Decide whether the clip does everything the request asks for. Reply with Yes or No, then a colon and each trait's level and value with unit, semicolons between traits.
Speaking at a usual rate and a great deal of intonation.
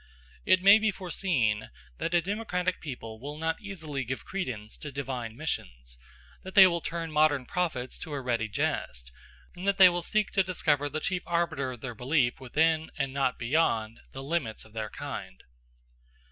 Yes: average, 175 wpm; wide, 6.2 semitones